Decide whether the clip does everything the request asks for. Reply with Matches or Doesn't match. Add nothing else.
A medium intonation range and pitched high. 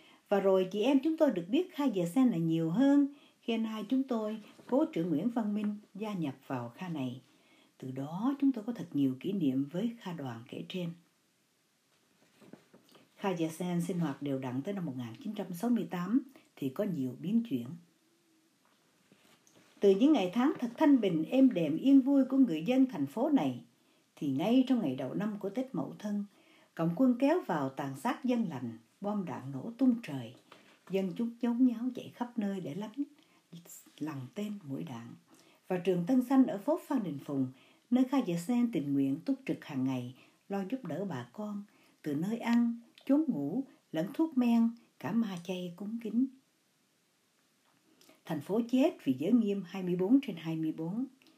Doesn't match